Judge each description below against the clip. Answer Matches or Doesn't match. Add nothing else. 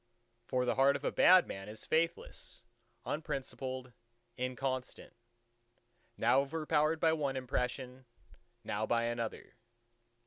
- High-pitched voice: Doesn't match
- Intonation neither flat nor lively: Matches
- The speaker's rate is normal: Doesn't match